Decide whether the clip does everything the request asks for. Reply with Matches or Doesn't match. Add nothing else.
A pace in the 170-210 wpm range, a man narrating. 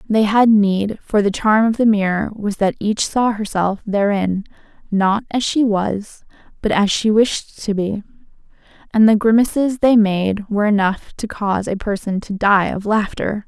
Doesn't match